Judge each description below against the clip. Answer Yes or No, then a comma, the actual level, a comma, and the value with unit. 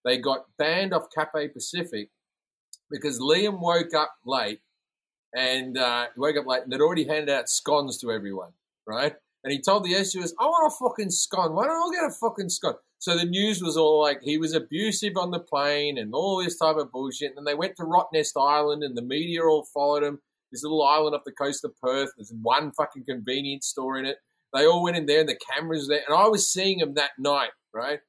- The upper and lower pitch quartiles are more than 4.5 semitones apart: No, average, 3.8 semitones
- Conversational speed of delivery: No, fast, 225 wpm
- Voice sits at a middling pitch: Yes, medium, 150 Hz